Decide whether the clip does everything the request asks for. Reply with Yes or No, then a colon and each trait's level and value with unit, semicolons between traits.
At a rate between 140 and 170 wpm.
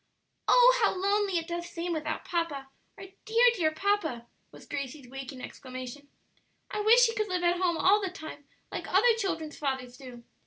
No: average, 180 wpm